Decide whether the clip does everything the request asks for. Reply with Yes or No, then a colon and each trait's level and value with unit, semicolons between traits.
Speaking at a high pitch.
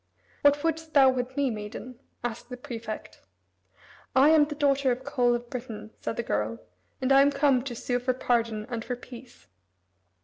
Yes: very high, 250 Hz